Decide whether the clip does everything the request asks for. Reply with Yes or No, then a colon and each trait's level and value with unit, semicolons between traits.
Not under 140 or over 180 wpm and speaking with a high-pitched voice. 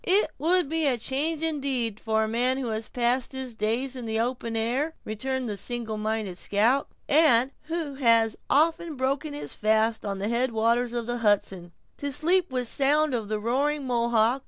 No: average, 190 wpm; high, 245 Hz